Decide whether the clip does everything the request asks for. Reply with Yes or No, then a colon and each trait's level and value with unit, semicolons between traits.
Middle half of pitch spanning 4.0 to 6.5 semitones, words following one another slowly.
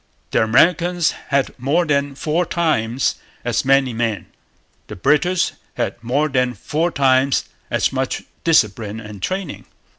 Yes: average, 5.3 semitones; slow, 130 wpm